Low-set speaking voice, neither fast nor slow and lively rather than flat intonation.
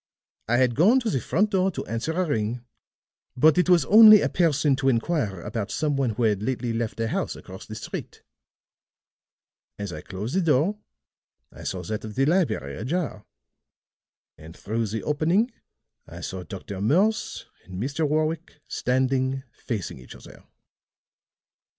Yes: low, 130 Hz; average, 160 wpm; wide, 7.1 semitones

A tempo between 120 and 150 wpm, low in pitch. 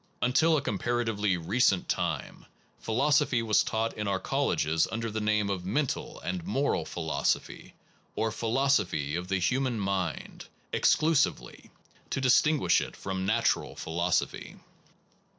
Yes: slow, 135 wpm; low, 110 Hz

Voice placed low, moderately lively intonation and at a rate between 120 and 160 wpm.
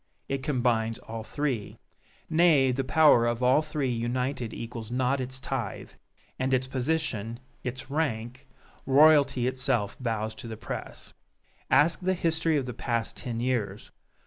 Yes: low, 130 Hz; average, 3.3 semitones; average, 145 wpm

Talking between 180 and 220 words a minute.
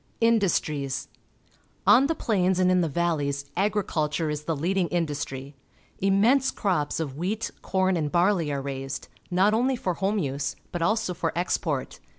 No: average, 160 wpm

